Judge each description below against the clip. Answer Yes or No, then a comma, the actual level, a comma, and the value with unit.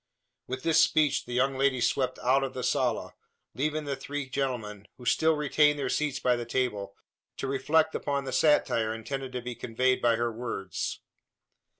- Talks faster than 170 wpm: Yes, average, 180 wpm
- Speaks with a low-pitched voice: Yes, low, 130 Hz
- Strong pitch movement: No, average, 2.9 semitones